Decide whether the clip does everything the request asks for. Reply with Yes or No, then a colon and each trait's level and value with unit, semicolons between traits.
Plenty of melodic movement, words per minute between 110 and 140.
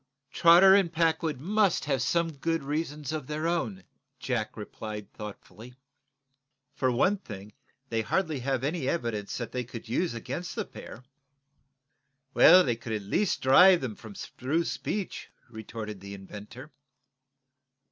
Yes: wide, 6.8 semitones; slow, 135 wpm